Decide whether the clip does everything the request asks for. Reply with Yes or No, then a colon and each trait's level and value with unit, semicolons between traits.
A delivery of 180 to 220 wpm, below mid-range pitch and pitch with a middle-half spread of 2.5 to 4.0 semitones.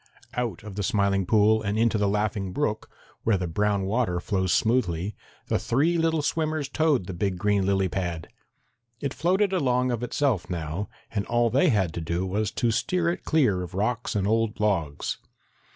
No: average, 185 wpm; low, 105 Hz; average, 4.8 semitones